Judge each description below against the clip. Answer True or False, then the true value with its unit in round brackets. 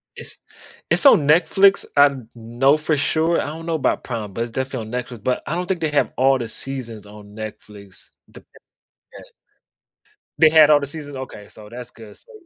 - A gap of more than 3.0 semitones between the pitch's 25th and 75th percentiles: True (5.2 semitones)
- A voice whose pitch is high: False (135 Hz)